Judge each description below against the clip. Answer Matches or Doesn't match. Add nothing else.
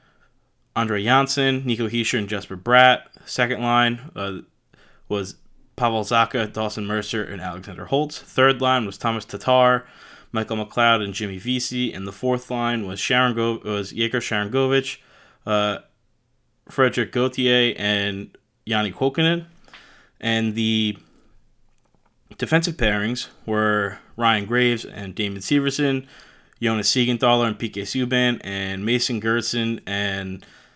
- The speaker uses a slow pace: Matches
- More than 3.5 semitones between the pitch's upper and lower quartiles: Doesn't match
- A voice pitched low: Matches